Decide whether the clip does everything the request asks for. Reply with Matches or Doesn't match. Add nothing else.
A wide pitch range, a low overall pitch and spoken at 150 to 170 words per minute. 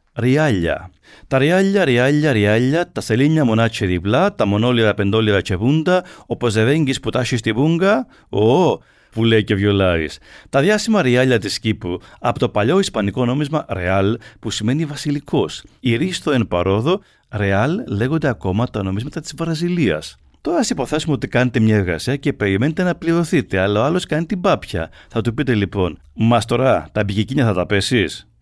Matches